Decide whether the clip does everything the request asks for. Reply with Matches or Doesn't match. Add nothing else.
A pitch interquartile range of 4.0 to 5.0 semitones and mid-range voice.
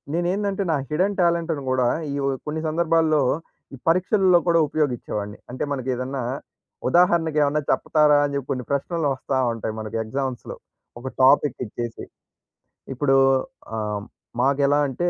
Matches